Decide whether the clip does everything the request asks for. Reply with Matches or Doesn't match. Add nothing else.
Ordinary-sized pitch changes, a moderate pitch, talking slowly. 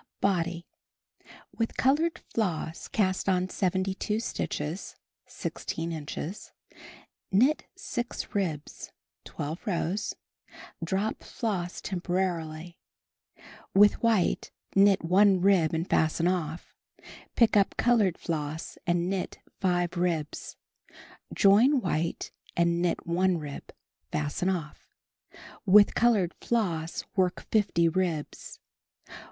Matches